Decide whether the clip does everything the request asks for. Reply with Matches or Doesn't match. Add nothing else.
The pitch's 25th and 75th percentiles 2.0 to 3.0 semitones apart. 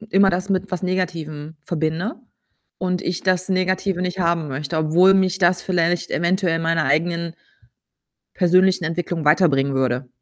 Matches